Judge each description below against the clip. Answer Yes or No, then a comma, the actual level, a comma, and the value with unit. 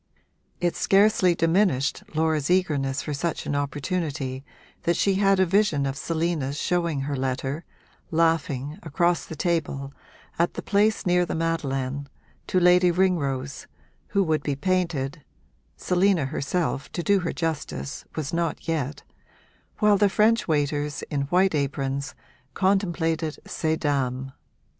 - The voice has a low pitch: No, medium, 160 Hz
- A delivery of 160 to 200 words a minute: No, slow, 135 wpm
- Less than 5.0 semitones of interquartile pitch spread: Yes, average, 4.2 semitones